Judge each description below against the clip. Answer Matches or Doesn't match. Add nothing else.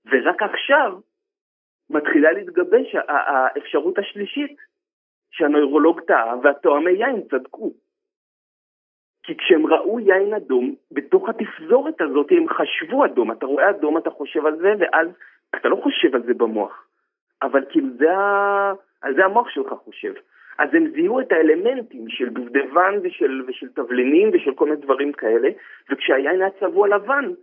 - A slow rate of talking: Doesn't match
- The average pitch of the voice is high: Matches